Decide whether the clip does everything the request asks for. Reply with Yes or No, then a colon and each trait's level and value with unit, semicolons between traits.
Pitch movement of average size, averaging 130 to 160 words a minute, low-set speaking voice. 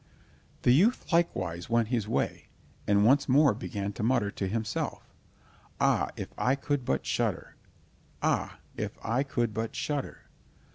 Yes: average, 4.9 semitones; average, 145 wpm; low, 120 Hz